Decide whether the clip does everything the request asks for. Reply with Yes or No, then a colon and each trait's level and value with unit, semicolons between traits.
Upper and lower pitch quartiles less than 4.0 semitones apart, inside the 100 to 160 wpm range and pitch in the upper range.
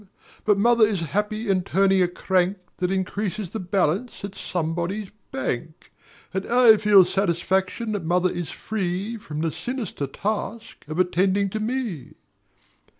Yes: average, 3.3 semitones; average, 145 wpm; high, 195 Hz